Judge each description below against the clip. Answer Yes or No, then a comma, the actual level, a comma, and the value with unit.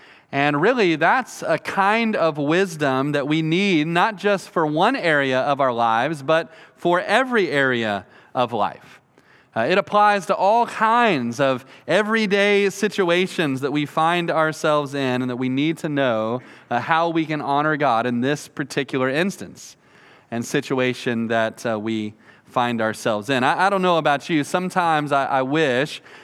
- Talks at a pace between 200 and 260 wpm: No, average, 165 wpm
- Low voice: No, medium, 150 Hz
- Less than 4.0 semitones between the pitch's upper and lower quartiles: No, average, 5.2 semitones